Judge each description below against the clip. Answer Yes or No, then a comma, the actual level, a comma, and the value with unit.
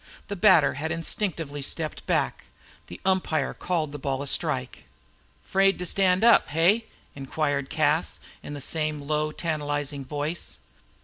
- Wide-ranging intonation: No, average, 3.3 semitones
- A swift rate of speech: No, average, 140 wpm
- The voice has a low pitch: No, medium, 155 Hz